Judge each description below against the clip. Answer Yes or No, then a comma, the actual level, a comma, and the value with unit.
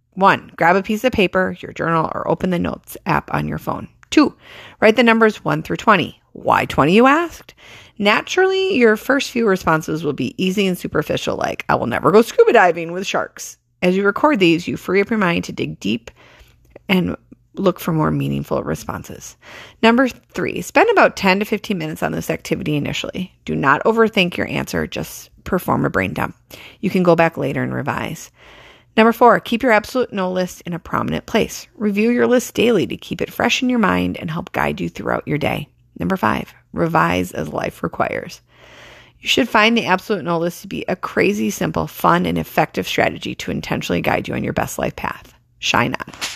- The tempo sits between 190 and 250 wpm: Yes, average, 200 wpm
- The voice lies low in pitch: No, medium, 185 Hz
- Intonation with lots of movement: Yes, wide, 6.4 semitones